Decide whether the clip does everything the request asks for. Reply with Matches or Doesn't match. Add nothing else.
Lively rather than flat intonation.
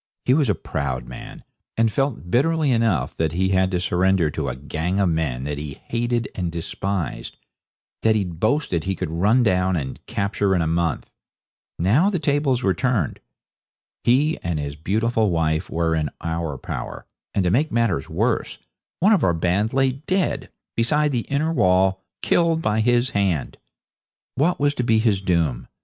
Matches